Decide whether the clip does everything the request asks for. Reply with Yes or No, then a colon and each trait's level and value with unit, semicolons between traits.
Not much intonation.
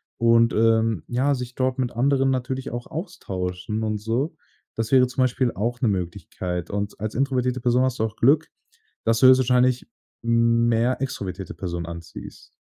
No: average, 3.1 semitones